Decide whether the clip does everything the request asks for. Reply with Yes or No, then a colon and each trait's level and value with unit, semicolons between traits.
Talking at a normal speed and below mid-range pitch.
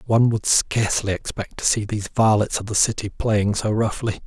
Yes: average, 195 wpm; low, 105 Hz